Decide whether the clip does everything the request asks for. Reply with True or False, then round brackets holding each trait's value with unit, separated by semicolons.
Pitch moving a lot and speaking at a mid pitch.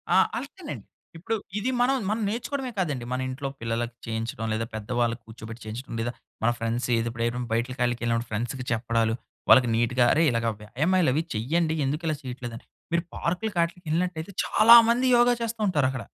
False (6.8 semitones; 125 Hz)